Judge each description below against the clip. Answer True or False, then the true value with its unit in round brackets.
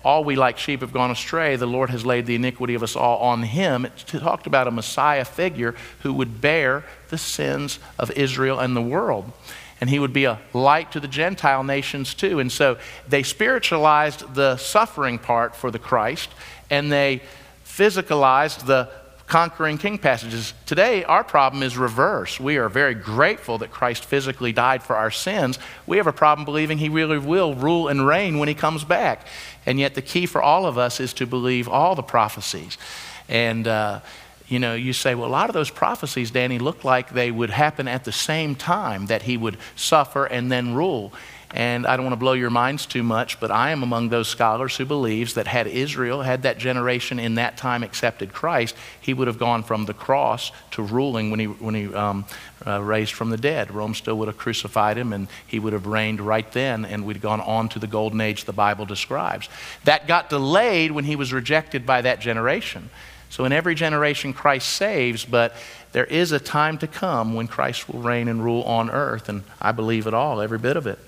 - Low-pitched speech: True (125 Hz)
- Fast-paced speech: True (210 wpm)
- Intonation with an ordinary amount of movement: True (3.8 semitones)